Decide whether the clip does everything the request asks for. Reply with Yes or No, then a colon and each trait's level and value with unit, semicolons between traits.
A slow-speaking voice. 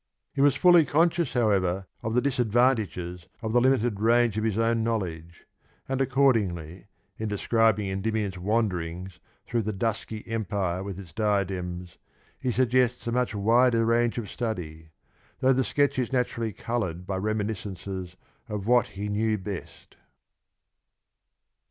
No: average, 145 wpm